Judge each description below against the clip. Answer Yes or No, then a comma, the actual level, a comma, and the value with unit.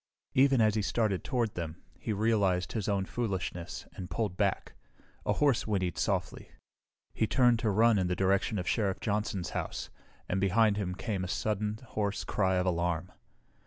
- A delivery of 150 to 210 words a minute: Yes, average, 170 wpm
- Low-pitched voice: Yes, low, 100 Hz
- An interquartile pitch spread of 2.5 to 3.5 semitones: Yes, average, 3.1 semitones